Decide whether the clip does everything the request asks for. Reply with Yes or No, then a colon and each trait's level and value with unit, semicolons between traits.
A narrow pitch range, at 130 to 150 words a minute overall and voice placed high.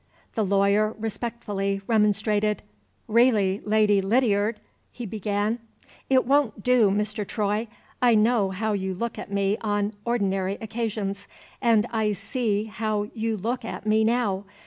Yes: narrow, 2.1 semitones; average, 140 wpm; high, 215 Hz